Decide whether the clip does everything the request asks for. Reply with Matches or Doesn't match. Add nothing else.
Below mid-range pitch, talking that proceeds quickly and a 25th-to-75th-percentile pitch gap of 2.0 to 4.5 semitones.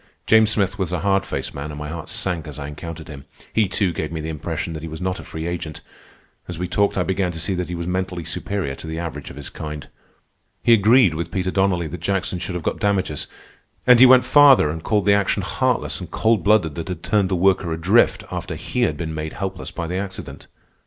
Matches